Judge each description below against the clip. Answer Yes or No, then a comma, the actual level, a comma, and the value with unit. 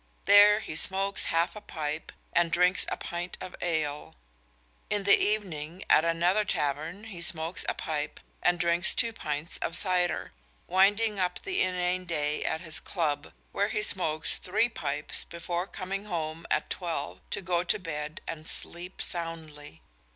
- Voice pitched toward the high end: No, medium, 175 Hz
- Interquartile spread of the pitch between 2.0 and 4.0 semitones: Yes, average, 3.3 semitones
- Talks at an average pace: Yes, average, 160 wpm